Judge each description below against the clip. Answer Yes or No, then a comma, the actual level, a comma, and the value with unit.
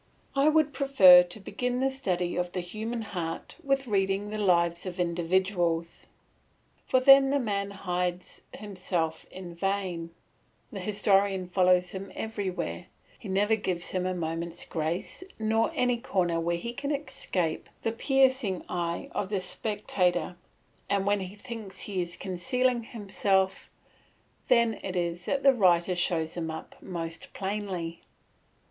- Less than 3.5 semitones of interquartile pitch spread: No, average, 4.0 semitones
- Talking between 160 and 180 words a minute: No, average, 145 wpm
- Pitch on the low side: No, high, 190 Hz